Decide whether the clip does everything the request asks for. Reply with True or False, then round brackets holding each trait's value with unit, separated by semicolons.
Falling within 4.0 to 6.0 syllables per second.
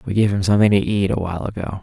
False (7.6 syllables/s)